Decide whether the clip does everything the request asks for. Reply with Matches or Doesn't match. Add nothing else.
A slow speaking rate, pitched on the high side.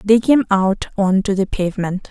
Doesn't match